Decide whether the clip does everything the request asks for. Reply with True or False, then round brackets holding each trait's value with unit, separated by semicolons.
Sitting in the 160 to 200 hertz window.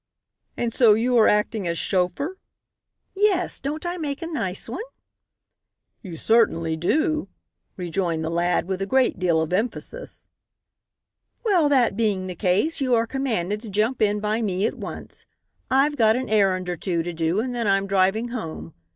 False (215 Hz)